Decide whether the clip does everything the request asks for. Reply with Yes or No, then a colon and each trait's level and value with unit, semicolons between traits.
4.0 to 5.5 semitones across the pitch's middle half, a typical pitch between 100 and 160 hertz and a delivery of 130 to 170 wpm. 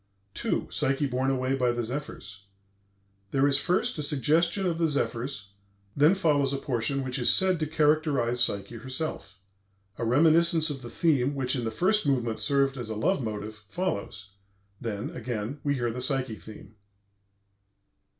Yes: average, 4.4 semitones; low, 135 Hz; average, 160 wpm